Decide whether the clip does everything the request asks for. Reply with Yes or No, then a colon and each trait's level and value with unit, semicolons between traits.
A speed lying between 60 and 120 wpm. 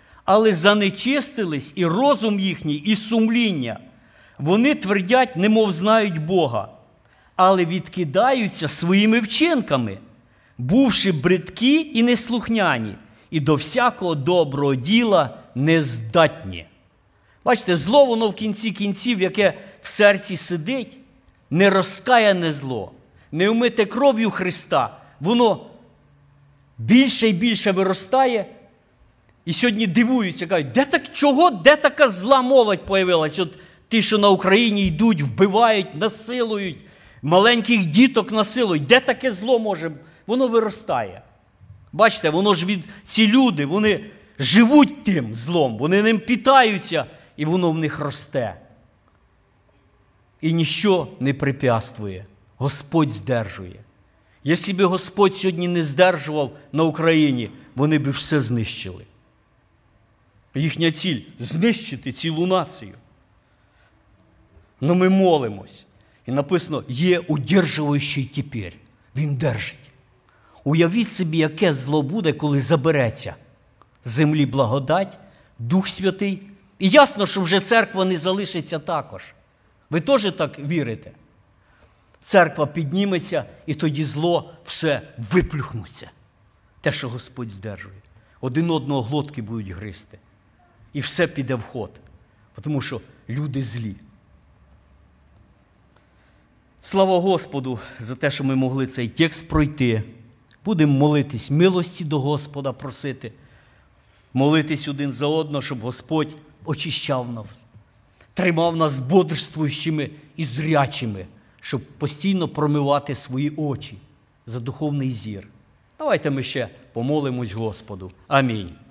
Yes: average, 110 wpm